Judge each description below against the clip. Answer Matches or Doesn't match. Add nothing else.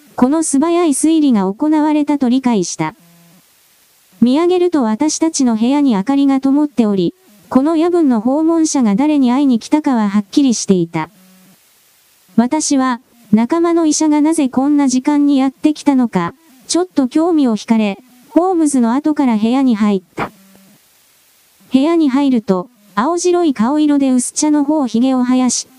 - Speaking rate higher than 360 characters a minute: Doesn't match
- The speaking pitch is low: Doesn't match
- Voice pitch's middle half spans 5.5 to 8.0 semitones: Doesn't match